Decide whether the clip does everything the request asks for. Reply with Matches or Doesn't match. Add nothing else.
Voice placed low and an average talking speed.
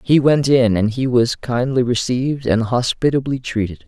Matches